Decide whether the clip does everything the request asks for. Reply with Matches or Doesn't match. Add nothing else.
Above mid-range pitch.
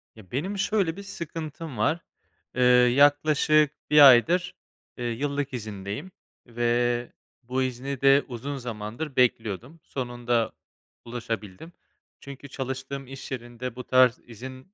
Doesn't match